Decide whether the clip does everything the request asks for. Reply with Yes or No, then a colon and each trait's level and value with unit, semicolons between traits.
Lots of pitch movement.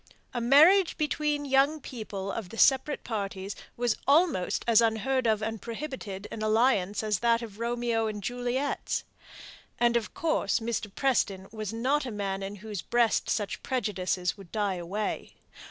No: average, 4.1 semitones